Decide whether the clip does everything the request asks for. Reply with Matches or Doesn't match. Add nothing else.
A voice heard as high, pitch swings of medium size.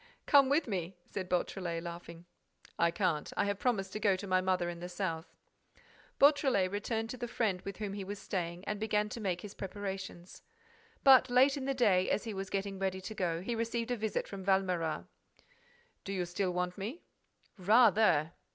Matches